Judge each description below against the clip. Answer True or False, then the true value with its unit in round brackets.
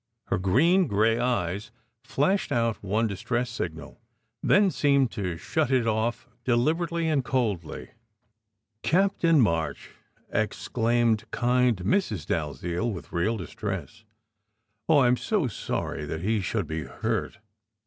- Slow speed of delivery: True (125 wpm)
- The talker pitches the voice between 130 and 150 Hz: False (115 Hz)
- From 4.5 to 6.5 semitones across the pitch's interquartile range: True (5.5 semitones)